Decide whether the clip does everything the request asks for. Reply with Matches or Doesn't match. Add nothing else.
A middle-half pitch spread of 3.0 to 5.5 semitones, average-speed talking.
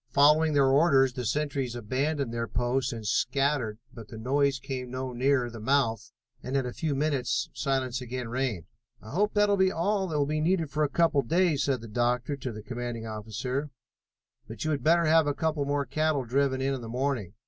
Doesn't match